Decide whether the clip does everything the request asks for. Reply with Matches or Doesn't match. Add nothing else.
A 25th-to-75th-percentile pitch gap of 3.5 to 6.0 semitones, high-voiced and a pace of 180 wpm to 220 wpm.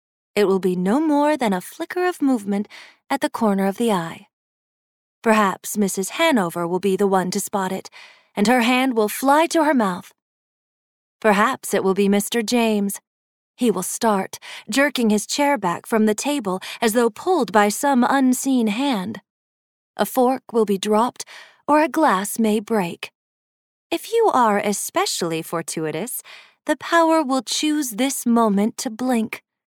Doesn't match